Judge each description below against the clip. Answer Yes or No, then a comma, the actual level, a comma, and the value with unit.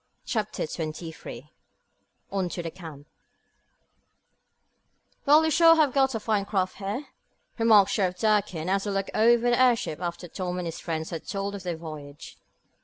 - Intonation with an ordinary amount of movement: Yes, average, 4.8 semitones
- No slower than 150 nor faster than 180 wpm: Yes, average, 160 wpm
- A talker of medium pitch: No, high, 195 Hz